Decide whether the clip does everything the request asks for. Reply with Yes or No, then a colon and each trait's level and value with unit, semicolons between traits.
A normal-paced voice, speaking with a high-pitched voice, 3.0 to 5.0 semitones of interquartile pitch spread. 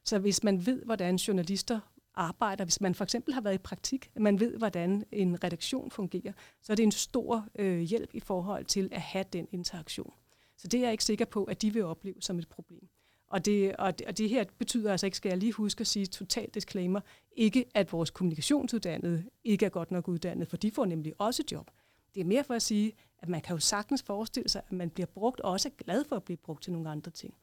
No: fast, 245 wpm; high, 200 Hz; average, 3.7 semitones